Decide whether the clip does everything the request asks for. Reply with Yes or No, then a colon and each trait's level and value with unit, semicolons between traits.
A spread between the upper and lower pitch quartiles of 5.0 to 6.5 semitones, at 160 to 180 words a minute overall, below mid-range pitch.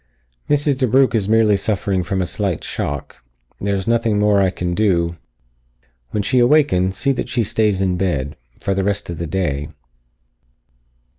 No: average, 3.8 semitones; average, 170 wpm; low, 100 Hz